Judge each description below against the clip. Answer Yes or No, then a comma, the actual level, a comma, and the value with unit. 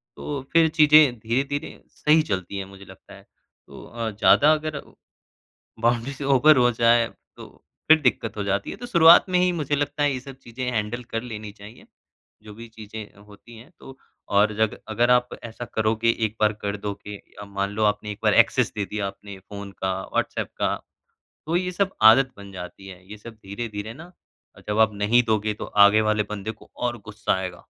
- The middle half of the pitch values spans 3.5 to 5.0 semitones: Yes, average, 4.2 semitones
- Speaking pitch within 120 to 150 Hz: No, low, 110 Hz